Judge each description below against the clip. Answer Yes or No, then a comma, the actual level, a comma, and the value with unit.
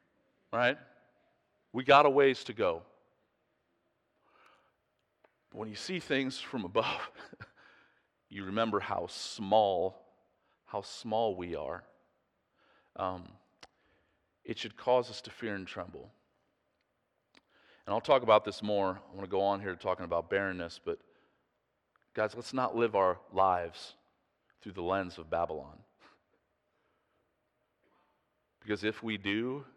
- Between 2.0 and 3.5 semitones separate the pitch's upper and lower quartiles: No, average, 4.2 semitones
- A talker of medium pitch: No, low, 105 Hz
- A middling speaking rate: No, slow, 125 wpm